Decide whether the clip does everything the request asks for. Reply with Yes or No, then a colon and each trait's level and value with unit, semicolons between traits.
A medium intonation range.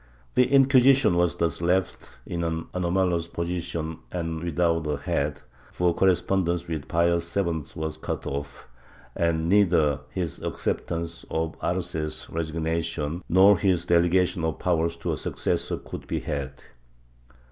No: narrow, 1.8 semitones